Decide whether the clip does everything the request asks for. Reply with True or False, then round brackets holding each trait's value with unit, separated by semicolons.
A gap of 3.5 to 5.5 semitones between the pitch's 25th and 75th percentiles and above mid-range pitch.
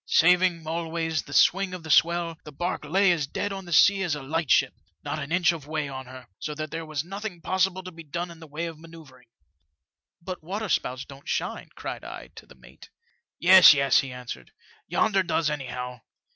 False (3.8 semitones; 165 Hz)